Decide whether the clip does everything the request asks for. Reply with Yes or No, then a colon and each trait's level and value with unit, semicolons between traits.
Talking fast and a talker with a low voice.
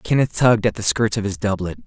Yes: fast, 260 wpm; low, 105 Hz